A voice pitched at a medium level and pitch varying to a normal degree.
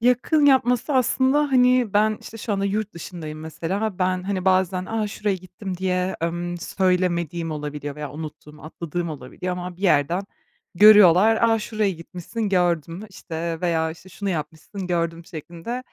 Yes: medium, 180 Hz; average, 4.0 semitones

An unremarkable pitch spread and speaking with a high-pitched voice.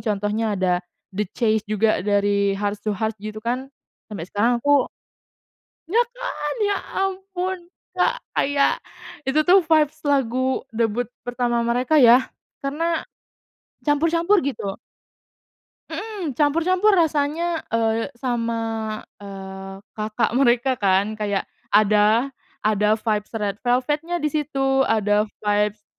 No: wide, 6.0 semitones; high, 240 Hz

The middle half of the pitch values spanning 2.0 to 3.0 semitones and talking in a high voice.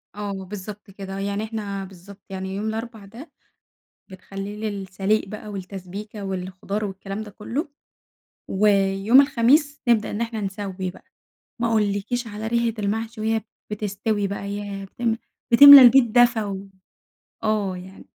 Yes: narrow, 2.4 semitones; high, 205 Hz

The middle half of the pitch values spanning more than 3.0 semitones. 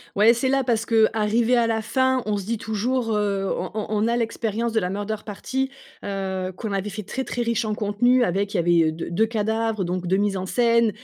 No: average, 2.7 semitones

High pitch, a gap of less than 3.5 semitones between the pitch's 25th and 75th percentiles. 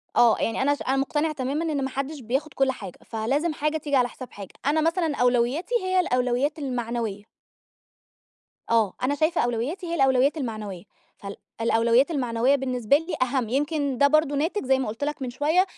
No: very high, 270 Hz; average, 3.8 semitones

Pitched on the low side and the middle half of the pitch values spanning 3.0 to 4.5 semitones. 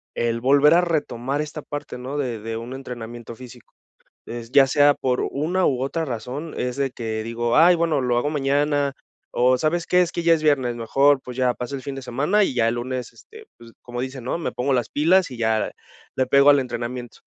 Yes: low, 130 Hz; average, 3.4 semitones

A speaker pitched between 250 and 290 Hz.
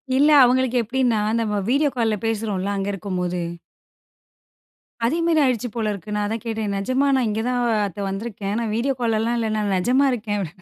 No: high, 225 Hz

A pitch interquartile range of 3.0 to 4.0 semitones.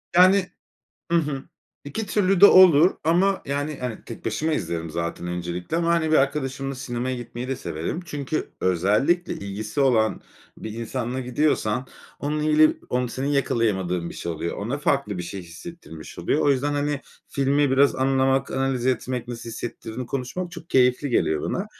No: average, 5.1 semitones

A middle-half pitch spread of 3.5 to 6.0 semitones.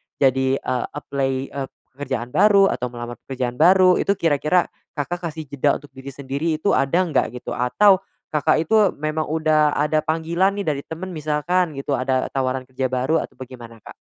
Yes: average, 3.9 semitones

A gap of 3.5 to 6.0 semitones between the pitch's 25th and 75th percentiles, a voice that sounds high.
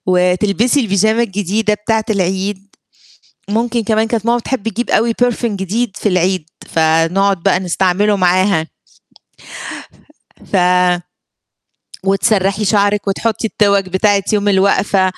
No: narrow, 2.6 semitones; high, 200 Hz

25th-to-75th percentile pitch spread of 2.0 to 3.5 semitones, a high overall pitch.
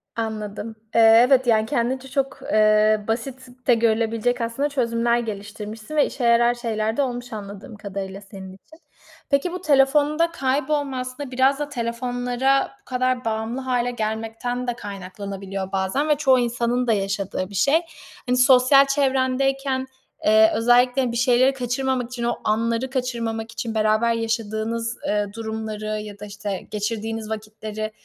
Yes: average, 3.1 semitones; high, 235 Hz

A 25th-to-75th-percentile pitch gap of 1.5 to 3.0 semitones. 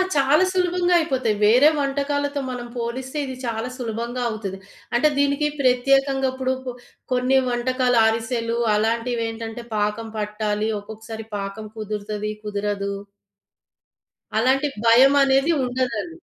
No: average, 3.6 semitones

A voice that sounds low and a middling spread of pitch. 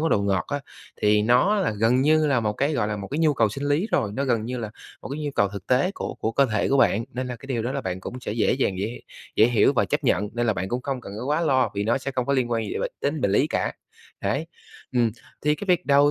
Yes: low, 125 Hz; average, 4.6 semitones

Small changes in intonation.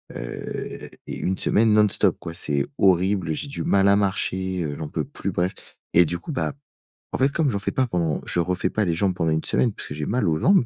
No: average, 4.2 semitones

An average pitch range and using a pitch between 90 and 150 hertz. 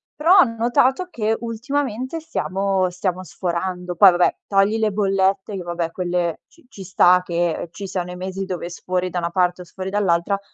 No: average, 3.3 semitones; high, 190 Hz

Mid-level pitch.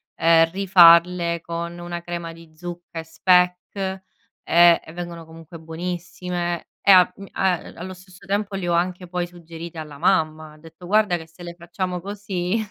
Yes: medium, 175 Hz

